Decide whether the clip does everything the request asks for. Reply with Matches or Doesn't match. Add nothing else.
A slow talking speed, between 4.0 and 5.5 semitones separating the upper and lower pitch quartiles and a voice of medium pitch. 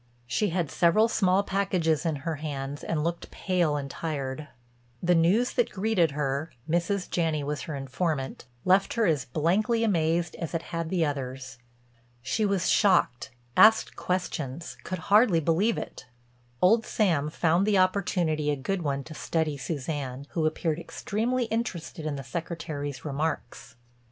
Doesn't match